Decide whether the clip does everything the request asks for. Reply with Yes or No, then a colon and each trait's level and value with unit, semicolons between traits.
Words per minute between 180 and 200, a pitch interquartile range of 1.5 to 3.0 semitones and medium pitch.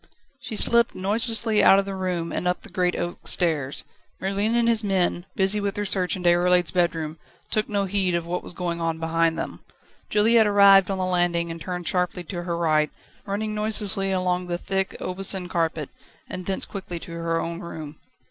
Yes: average, 195 wpm; average, 2.7 semitones; medium, 180 Hz